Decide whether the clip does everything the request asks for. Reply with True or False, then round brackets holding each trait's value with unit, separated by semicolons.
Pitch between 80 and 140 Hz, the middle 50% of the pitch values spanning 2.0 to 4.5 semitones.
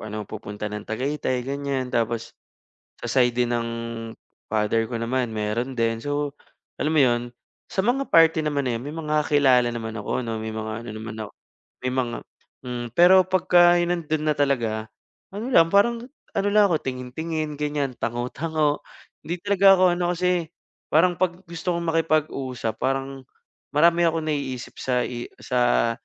False (135 Hz; 5.5 semitones)